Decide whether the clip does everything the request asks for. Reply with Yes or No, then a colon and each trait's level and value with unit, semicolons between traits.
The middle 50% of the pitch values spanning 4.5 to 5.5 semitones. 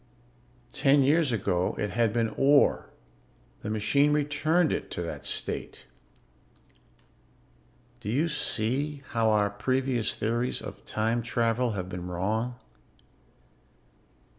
Yes: average, 4.8 semitones